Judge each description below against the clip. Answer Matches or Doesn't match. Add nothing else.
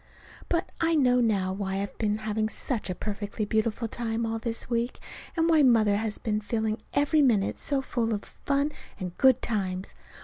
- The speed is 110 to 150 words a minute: Doesn't match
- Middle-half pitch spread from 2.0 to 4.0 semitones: Matches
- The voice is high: Matches